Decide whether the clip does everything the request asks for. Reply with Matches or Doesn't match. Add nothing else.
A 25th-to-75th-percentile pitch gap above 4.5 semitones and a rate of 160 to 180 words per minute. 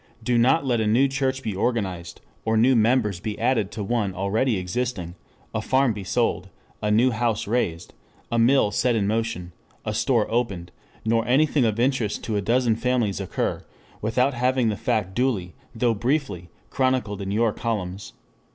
Doesn't match